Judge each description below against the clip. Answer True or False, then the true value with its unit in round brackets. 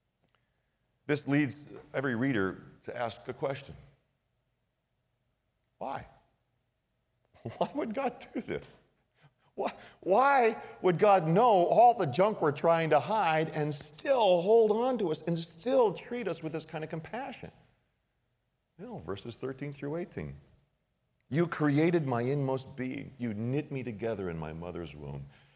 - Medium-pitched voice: True (145 Hz)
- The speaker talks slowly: False (145 wpm)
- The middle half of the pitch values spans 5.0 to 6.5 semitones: True (5.6 semitones)